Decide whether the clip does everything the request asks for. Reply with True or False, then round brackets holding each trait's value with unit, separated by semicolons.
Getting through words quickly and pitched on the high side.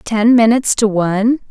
False (160 wpm; 220 Hz)